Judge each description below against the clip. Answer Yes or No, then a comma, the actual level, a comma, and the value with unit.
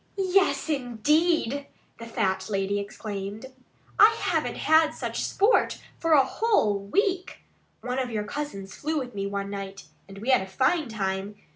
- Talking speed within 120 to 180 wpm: Yes, average, 155 wpm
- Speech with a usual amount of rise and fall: No, wide, 7.9 semitones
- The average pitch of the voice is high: Yes, high, 235 Hz